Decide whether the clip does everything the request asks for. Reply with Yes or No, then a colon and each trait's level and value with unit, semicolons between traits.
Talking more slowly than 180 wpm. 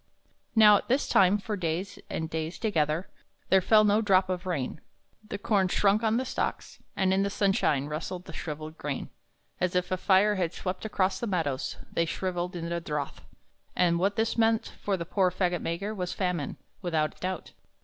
No: average, 190 wpm